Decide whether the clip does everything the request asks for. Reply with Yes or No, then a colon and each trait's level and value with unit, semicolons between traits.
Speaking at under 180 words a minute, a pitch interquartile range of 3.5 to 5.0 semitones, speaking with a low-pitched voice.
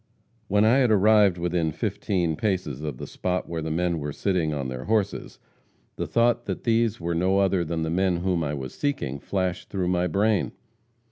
No: average, 195 wpm; average, 4.0 semitones; very low, 90 Hz